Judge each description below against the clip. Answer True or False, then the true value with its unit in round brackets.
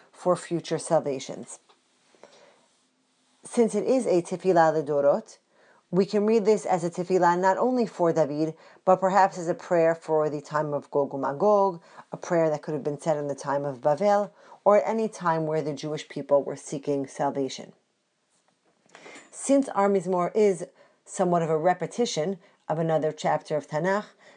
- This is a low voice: False (170 Hz)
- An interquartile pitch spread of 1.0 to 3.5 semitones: False (4.5 semitones)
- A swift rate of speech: False (165 wpm)